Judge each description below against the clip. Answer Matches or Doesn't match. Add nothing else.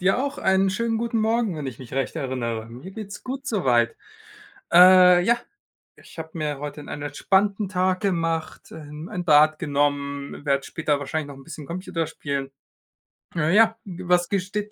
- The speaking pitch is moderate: Matches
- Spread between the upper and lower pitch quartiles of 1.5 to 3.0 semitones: Doesn't match